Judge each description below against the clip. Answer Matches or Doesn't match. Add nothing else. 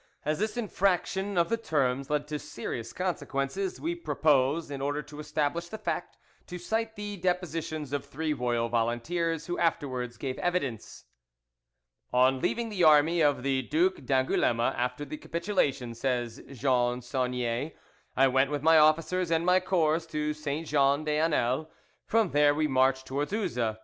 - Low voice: Doesn't match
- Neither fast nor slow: Matches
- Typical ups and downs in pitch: Matches